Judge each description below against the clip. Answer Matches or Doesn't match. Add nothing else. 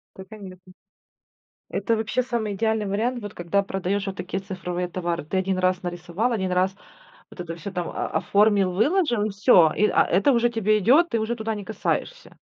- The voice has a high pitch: Matches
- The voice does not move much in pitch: Doesn't match